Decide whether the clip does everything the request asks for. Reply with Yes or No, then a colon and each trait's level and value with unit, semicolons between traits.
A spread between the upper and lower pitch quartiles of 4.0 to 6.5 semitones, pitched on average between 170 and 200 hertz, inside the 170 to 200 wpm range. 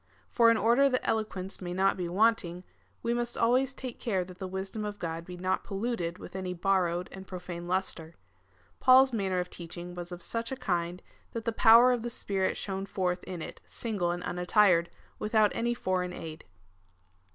Yes: average, 4.4 semitones; high, 190 Hz; average, 190 wpm